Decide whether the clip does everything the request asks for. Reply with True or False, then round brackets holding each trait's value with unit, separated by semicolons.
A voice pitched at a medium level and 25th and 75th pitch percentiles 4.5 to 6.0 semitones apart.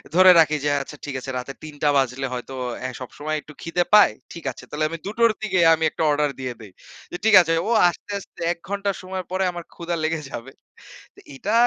True (160 Hz; 5.2 semitones)